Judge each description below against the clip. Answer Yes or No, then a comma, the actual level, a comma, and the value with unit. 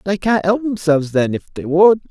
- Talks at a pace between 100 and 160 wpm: No, fast, 230 wpm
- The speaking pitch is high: No, medium, 180 Hz